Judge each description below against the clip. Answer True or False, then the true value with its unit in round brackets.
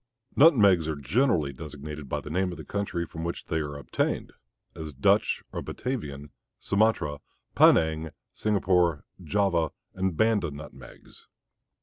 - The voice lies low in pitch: True (80 Hz)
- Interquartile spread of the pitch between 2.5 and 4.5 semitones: False (5.2 semitones)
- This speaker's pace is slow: True (130 wpm)